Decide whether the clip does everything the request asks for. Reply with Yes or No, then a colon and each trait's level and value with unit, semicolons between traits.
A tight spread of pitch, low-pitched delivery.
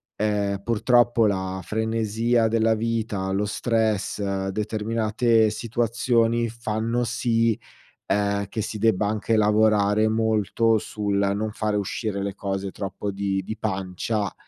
Yes: narrow, 2.1 semitones; low, 110 Hz